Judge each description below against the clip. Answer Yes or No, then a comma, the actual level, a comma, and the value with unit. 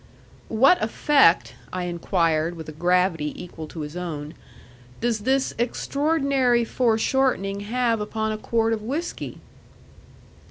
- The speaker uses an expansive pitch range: Yes, wide, 6.3 semitones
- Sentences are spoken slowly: Yes, slow, 120 wpm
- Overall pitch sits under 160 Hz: No, high, 215 Hz